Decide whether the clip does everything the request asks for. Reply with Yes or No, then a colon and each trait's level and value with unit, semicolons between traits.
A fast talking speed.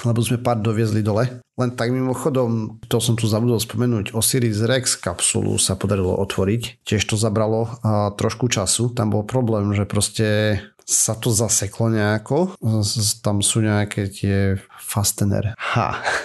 No: average, 150 wpm